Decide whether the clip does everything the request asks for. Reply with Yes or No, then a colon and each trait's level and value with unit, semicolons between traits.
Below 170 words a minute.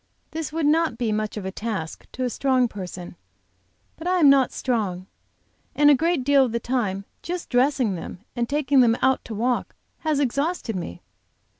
No: average, 185 wpm